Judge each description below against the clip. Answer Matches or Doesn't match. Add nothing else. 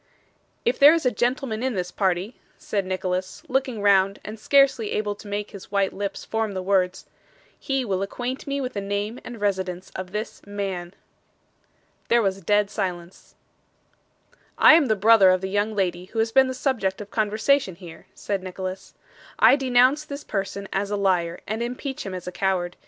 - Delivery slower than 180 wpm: Doesn't match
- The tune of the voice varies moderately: Matches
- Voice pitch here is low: Doesn't match